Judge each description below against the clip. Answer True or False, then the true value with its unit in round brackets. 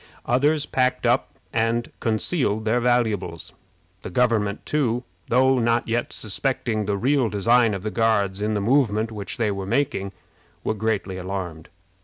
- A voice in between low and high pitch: False (110 Hz)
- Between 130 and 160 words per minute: True (150 wpm)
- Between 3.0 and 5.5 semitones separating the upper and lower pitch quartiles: True (3.3 semitones)